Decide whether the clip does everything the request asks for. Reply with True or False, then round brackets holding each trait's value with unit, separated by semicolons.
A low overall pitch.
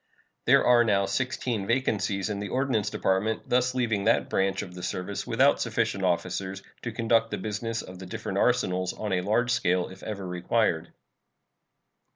True (100 Hz)